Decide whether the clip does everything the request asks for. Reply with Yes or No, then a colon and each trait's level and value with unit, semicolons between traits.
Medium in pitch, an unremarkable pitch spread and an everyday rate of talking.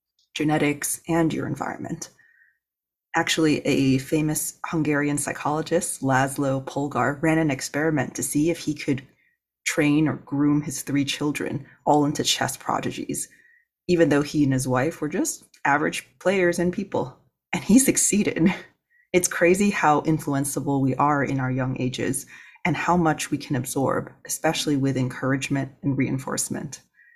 Yes: medium, 150 Hz; average, 3.2 semitones; average, 145 wpm